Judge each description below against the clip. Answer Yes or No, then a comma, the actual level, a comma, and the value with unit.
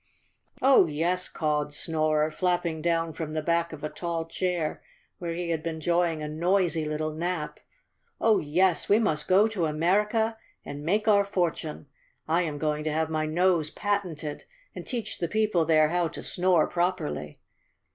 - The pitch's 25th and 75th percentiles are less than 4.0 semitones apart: Yes, average, 2.8 semitones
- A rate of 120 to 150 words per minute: No, average, 165 wpm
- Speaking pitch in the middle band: Yes, medium, 165 Hz